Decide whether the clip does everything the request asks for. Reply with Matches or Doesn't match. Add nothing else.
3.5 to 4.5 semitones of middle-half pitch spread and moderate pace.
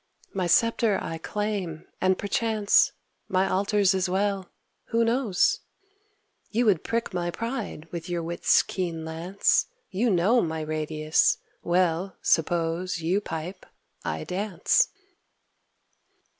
Doesn't match